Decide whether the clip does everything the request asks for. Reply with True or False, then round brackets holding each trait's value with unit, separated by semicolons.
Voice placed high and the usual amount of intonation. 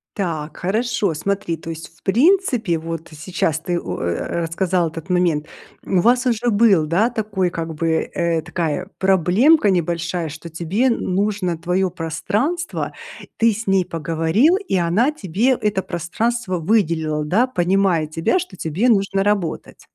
False (180 Hz; 4.6 semitones)